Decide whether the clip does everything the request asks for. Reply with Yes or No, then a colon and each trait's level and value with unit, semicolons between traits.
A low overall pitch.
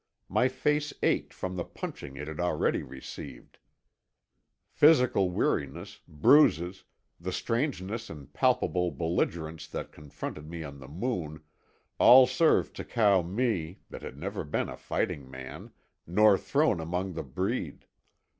Yes: very low, 90 Hz